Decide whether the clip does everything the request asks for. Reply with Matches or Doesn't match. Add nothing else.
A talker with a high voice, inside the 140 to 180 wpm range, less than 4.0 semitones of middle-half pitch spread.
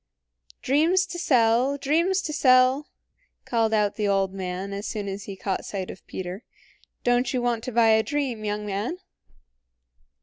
Doesn't match